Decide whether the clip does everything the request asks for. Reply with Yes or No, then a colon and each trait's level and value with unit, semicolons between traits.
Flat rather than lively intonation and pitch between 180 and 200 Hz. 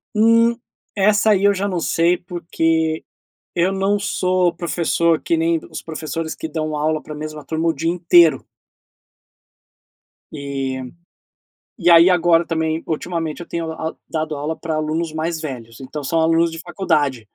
No: narrow, 2.0 semitones; medium, 165 Hz